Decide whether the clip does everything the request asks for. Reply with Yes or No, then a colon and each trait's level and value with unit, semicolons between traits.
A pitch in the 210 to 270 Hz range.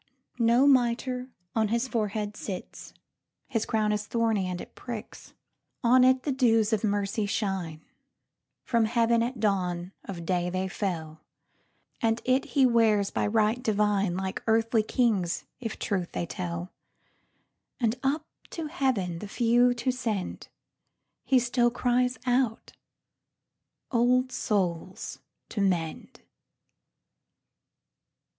Yes: high, 220 Hz